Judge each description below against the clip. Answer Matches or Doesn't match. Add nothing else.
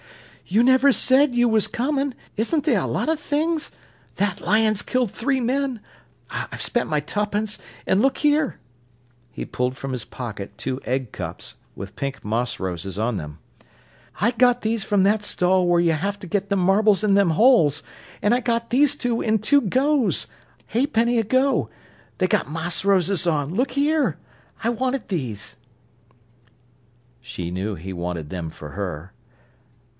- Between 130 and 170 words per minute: Matches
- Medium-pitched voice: Doesn't match